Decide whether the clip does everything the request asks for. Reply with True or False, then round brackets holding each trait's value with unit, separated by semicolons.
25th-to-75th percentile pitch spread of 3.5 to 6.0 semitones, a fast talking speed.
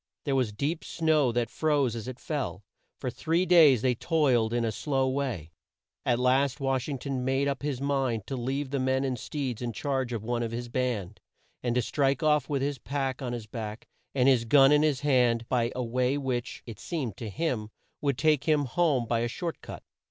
False (3.1 semitones; 220 wpm)